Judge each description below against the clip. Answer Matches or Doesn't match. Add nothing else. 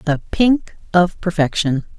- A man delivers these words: Doesn't match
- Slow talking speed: Matches